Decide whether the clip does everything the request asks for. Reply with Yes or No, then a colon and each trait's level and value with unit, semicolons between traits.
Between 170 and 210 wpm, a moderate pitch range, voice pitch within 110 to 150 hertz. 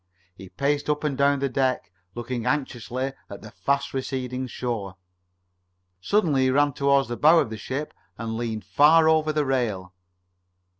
No: average, 160 wpm; average, 3.4 semitones; low, 135 Hz